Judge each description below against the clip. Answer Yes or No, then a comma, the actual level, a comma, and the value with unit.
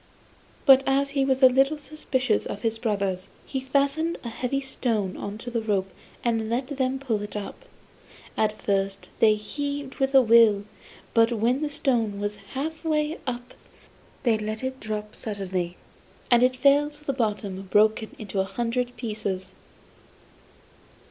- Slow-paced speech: No, average, 160 wpm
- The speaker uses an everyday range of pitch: Yes, average, 4.3 semitones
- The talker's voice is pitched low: No, high, 235 Hz